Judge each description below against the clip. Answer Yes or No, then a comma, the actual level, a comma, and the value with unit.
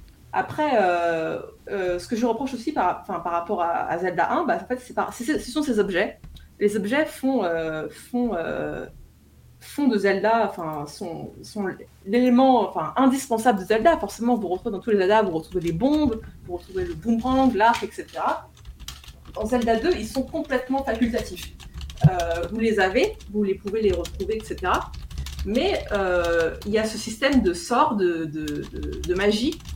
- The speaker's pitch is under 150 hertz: No, high, 210 Hz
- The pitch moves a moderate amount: No, wide, 6.4 semitones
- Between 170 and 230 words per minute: Yes, average, 180 wpm